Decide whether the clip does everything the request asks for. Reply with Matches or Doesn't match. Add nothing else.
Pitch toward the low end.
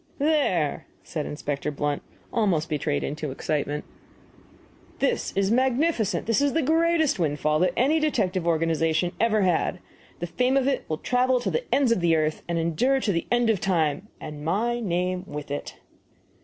Doesn't match